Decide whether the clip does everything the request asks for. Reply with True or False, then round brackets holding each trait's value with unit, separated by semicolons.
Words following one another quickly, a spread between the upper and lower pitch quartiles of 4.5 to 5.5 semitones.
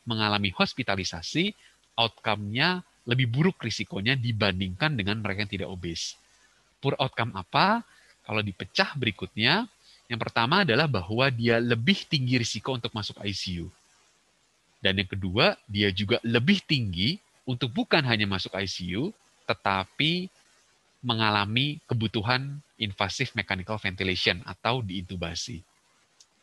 False (110 wpm; 5.1 semitones)